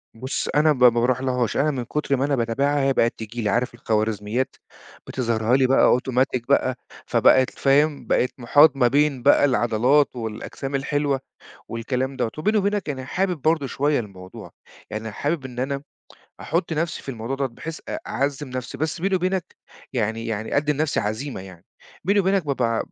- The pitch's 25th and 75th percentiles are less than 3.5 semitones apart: No, average, 3.8 semitones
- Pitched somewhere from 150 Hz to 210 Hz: No, low, 130 Hz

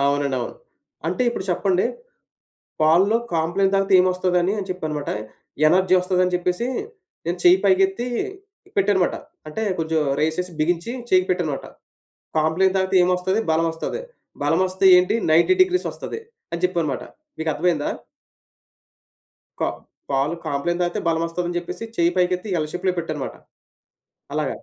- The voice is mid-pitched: Yes, medium, 180 Hz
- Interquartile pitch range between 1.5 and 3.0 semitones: Yes, narrow, 2.6 semitones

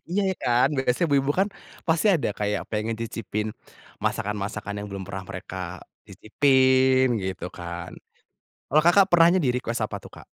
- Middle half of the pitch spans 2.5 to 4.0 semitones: No, wide, 5.5 semitones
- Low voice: Yes, low, 120 Hz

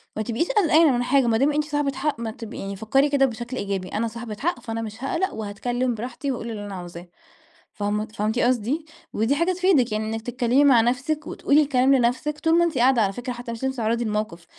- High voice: Yes, high, 245 Hz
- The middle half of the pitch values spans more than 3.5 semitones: Yes, average, 4.1 semitones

